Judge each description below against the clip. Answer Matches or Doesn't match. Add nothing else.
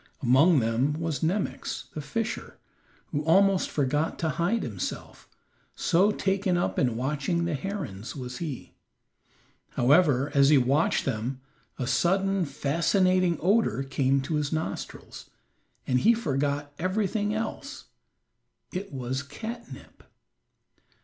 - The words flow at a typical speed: Doesn't match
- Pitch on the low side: Doesn't match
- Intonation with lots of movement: Matches